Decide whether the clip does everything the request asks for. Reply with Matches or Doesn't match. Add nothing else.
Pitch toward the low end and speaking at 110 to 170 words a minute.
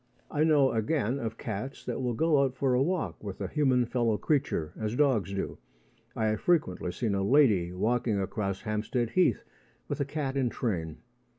Doesn't match